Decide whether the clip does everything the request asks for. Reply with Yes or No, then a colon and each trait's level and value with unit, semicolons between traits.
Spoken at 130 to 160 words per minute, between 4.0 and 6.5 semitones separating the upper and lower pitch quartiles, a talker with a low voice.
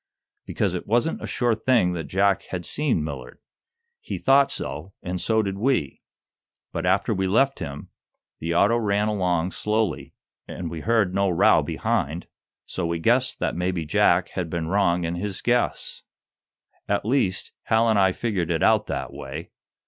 No: average, 170 wpm; average, 4.6 semitones; very low, 95 Hz